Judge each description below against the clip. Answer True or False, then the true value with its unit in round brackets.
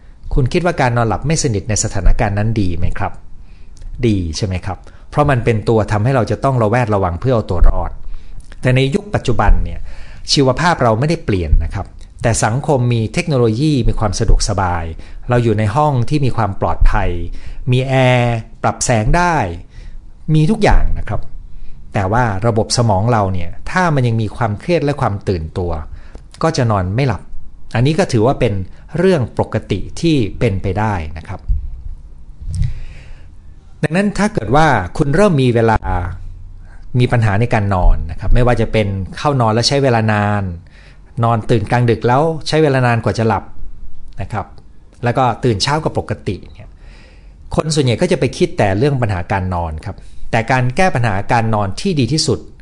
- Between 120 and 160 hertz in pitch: False (110 Hz)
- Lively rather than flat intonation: True (6.2 semitones)